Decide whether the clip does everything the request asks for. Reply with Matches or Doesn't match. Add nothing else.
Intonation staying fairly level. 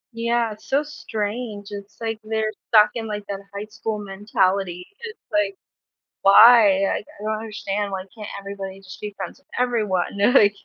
Matches